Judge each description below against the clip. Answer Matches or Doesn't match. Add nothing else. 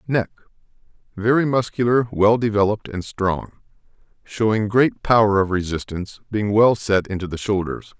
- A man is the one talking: Matches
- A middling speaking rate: Doesn't match